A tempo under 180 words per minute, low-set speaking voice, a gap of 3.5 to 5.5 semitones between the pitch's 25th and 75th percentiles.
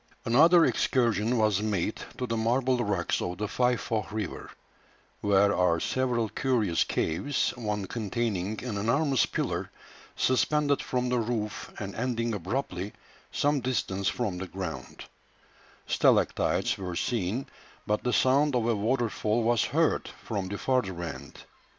Yes: average, 140 wpm; low, 115 Hz; average, 4.0 semitones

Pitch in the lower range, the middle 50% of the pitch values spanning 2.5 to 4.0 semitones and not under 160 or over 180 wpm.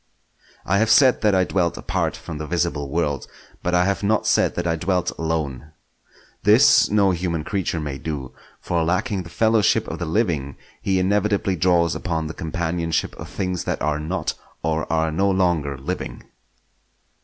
Yes: very low, 85 Hz; average, 3.3 semitones; average, 170 wpm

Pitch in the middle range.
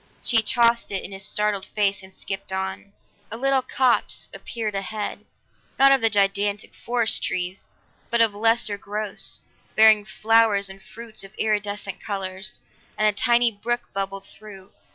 No: high, 210 Hz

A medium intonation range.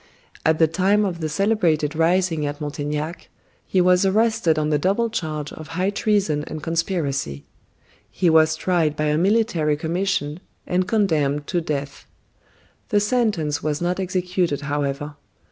Yes: average, 3.9 semitones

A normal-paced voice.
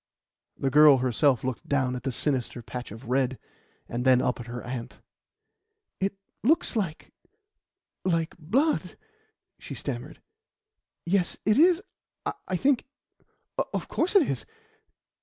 No: slow, 130 wpm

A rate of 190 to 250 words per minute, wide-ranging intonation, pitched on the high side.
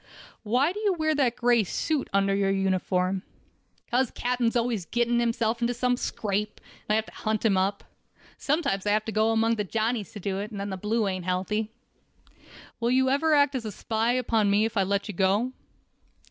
No: average, 200 wpm; average, 3.5 semitones; high, 220 Hz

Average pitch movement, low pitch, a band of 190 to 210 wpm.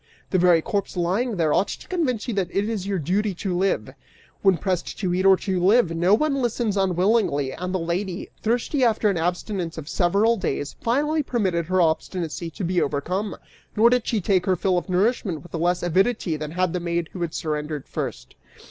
No: average, 3.6 semitones; medium, 185 Hz; average, 200 wpm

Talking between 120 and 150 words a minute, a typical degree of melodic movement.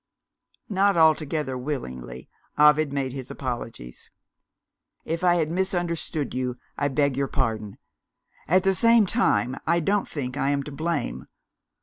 Yes: slow, 135 wpm; average, 4.9 semitones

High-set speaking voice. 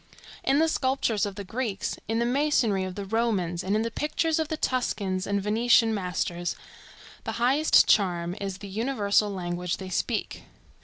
Yes: high, 210 Hz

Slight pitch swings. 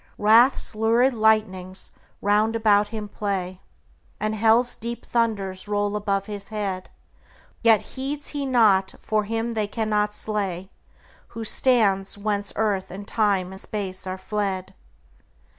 Yes: narrow, 2.3 semitones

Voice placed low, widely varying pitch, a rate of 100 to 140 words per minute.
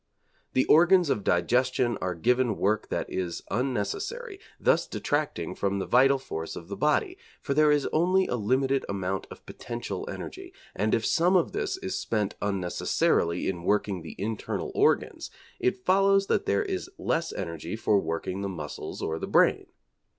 No: low, 120 Hz; wide, 8.3 semitones; average, 165 wpm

